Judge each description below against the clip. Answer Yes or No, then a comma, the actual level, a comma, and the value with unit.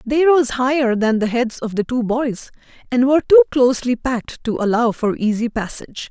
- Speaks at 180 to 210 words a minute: Yes, average, 195 wpm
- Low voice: No, very high, 250 Hz